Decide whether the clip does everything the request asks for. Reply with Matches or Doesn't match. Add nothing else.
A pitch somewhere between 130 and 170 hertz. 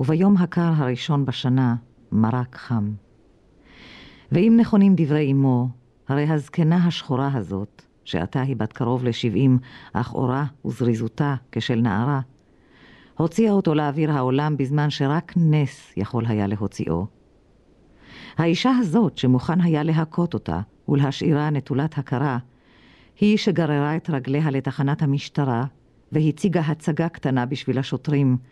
Matches